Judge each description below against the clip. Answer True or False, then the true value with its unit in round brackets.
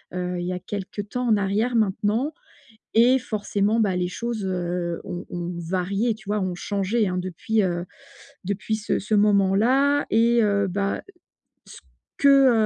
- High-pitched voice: True (200 Hz)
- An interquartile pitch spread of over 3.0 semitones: True (3.5 semitones)